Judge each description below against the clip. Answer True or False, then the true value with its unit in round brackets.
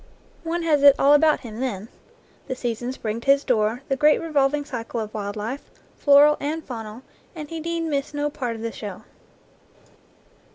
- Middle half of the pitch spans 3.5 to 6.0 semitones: True (4.6 semitones)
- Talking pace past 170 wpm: True (180 wpm)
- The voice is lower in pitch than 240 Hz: False (275 Hz)